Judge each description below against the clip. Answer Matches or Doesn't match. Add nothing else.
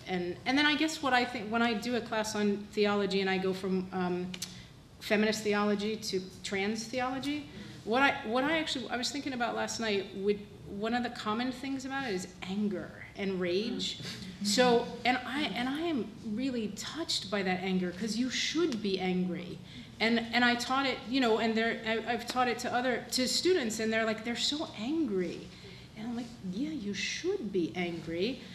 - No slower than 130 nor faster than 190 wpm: Doesn't match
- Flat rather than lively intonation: Doesn't match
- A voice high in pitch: Matches